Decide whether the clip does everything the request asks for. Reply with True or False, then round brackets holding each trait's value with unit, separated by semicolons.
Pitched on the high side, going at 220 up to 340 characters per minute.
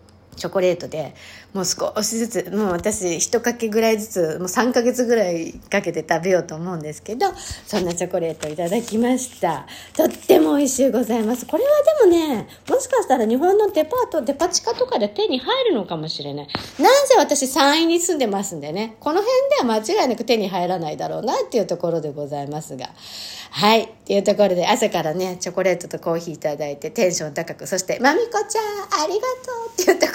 False (220 Hz; 430 characters per minute)